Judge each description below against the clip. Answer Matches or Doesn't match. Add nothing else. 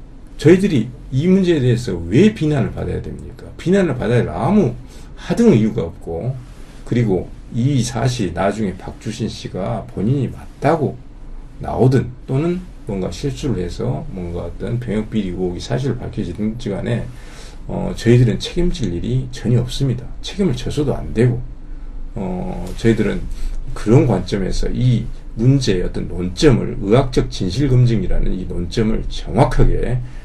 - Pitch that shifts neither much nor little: Matches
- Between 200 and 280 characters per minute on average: Doesn't match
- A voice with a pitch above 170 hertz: Doesn't match